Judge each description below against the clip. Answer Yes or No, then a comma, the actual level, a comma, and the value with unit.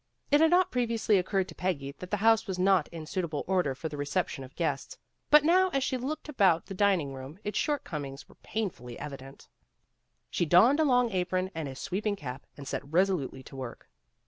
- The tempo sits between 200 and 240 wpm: Yes, fast, 205 wpm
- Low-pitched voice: No, medium, 185 Hz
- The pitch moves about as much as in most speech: No, wide, 7.7 semitones